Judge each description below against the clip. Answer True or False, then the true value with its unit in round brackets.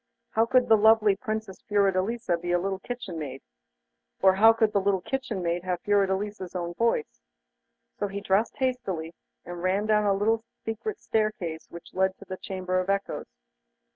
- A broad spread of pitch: False (3.1 semitones)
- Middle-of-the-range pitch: False (200 Hz)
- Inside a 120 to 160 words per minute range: False (170 wpm)